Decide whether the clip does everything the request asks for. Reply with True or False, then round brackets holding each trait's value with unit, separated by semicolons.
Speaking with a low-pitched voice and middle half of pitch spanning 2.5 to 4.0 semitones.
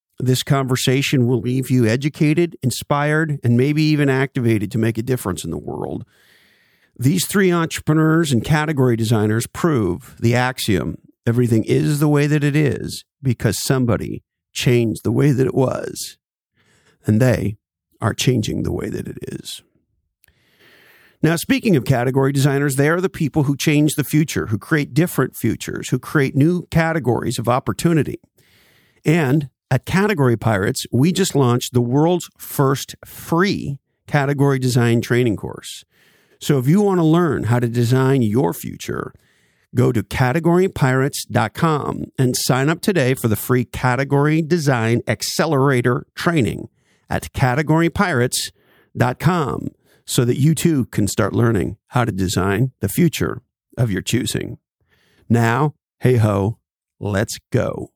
False (130 Hz; 4.4 semitones)